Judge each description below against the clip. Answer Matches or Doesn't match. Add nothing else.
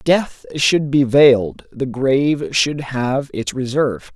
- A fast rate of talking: Doesn't match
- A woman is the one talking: Doesn't match